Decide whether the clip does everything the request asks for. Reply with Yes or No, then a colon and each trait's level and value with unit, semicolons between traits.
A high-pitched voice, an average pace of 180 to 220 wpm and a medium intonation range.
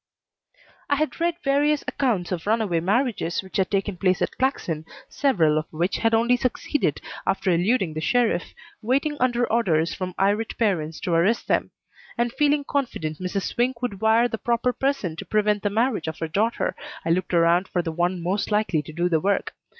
No: high, 205 Hz; average, 190 wpm; wide, 5.8 semitones